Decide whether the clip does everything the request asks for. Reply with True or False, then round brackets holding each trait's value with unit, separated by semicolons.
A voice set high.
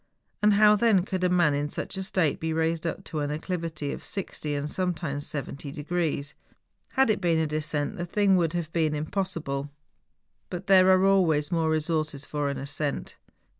False (160 Hz)